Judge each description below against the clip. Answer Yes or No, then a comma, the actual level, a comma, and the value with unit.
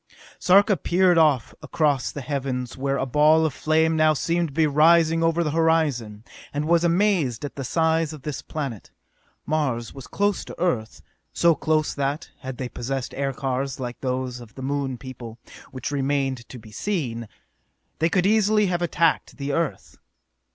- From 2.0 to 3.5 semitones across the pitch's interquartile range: No, average, 4.0 semitones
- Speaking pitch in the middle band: Yes, medium, 145 Hz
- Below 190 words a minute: Yes, average, 170 wpm